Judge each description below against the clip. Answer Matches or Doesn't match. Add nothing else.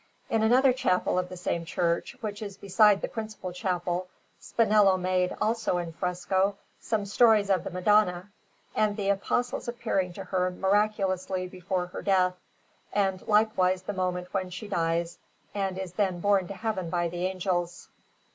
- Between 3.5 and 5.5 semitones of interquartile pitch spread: Doesn't match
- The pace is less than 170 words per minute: Matches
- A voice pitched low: Doesn't match